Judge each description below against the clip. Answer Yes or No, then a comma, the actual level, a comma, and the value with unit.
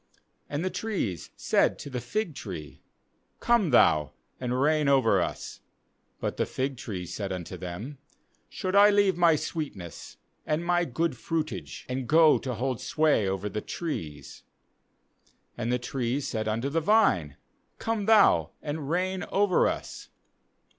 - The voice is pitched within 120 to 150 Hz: Yes, medium, 140 Hz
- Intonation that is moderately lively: No, wide, 7.8 semitones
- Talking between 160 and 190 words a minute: No, average, 145 wpm